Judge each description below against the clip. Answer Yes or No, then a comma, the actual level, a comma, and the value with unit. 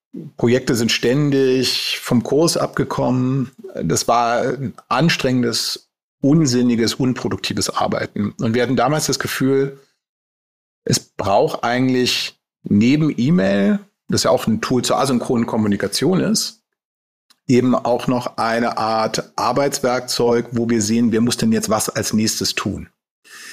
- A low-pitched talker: Yes, low, 125 Hz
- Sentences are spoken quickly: No, slow, 125 wpm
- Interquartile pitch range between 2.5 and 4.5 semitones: Yes, average, 2.9 semitones